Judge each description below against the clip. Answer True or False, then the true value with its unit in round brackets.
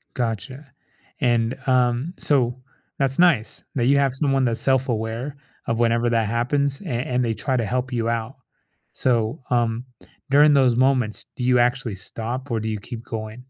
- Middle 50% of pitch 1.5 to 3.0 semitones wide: True (2.5 semitones)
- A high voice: False (125 Hz)